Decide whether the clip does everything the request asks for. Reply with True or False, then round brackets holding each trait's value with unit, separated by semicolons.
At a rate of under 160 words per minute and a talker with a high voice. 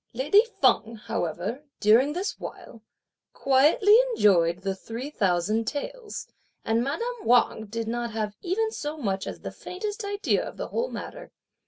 True (150 wpm; 250 Hz)